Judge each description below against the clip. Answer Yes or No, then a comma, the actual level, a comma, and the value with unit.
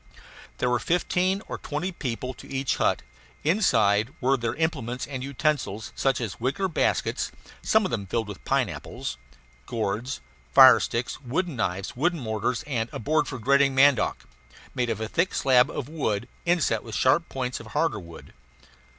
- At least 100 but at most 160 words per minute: No, average, 170 wpm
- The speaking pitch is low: Yes, low, 130 Hz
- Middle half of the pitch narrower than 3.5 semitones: No, average, 4.8 semitones